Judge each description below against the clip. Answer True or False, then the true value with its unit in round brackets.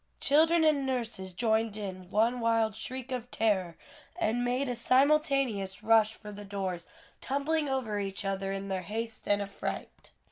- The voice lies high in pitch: True (225 Hz)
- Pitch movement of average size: True (4.7 semitones)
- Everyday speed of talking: True (155 wpm)